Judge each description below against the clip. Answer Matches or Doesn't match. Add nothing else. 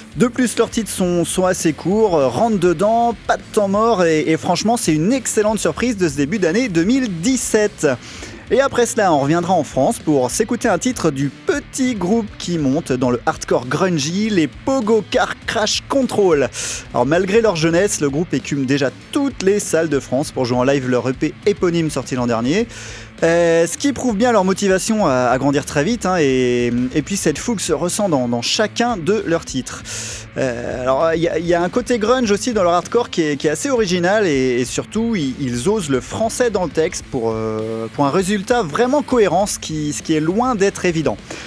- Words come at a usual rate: Matches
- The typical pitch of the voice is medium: Matches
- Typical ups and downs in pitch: Doesn't match